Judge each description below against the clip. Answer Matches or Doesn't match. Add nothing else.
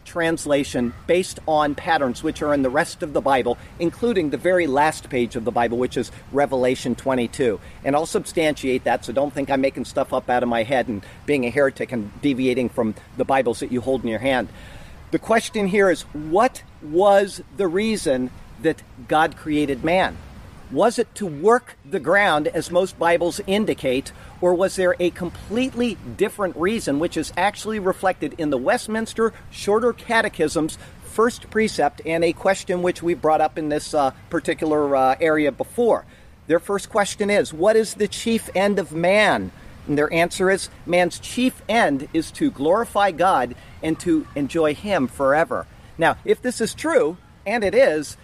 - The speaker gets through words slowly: Doesn't match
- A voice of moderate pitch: Matches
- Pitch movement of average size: Doesn't match